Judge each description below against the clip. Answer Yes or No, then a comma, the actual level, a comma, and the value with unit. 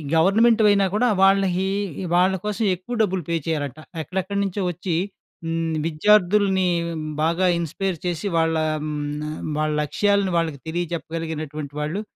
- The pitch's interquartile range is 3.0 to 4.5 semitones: Yes, average, 3.6 semitones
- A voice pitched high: No, medium, 175 Hz